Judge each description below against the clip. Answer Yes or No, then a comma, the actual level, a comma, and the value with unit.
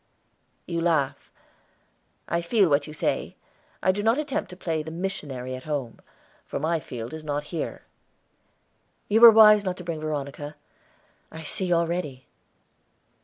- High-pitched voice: No, medium, 160 Hz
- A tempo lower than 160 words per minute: Yes, average, 150 wpm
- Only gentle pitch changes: No, average, 4.1 semitones